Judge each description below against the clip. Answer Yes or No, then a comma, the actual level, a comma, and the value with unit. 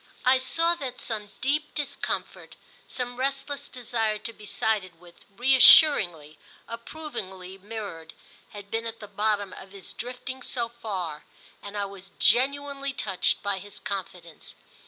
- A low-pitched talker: No, high, 220 Hz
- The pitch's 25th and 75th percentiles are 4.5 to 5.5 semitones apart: Yes, average, 4.9 semitones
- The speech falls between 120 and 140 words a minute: Yes, slow, 135 wpm